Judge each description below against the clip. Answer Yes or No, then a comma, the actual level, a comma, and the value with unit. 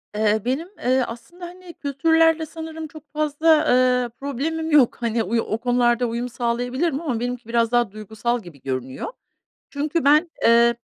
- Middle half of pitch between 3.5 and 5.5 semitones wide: Yes, average, 4.9 semitones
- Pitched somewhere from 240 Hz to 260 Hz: Yes, very high, 250 Hz